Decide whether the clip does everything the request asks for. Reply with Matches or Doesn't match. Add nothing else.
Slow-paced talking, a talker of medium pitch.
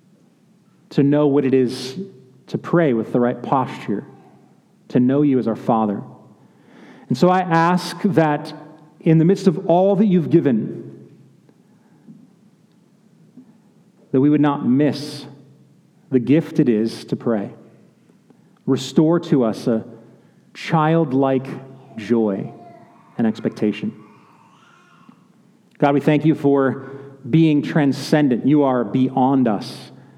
Matches